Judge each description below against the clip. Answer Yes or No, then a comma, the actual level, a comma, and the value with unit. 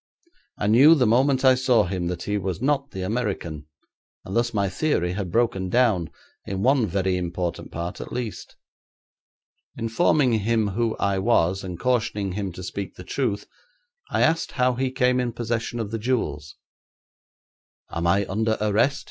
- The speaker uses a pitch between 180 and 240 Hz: No, low, 110 Hz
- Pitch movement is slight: No, average, 4.8 semitones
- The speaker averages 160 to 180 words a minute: Yes, average, 165 wpm